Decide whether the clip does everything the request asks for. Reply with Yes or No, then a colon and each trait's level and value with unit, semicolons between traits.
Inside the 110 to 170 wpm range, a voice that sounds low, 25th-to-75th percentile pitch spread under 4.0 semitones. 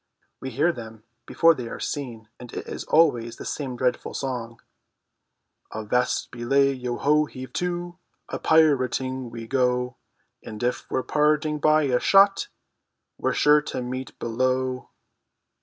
Yes: average, 140 wpm; low, 130 Hz; average, 3.6 semitones